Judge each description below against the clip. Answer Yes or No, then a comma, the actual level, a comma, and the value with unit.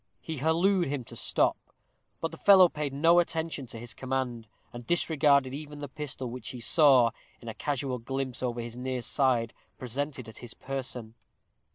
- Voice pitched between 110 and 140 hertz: Yes, low, 135 Hz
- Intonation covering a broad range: No, average, 3.6 semitones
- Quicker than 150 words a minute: Yes, average, 180 wpm